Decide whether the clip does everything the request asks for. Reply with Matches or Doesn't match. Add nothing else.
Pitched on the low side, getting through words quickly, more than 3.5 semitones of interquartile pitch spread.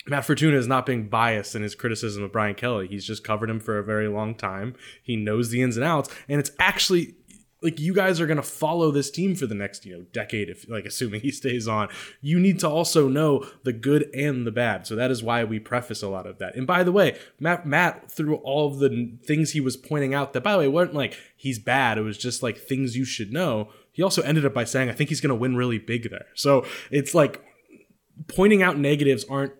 Matches